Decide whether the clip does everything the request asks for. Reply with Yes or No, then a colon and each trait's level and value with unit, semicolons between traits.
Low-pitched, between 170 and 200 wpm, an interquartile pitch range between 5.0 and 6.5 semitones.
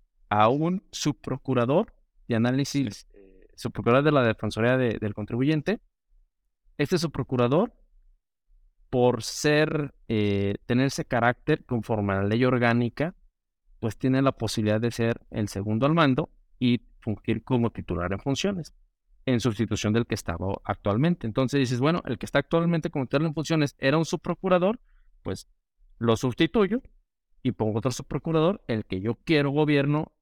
No: low, 125 Hz; average, 145 wpm; wide, 5.4 semitones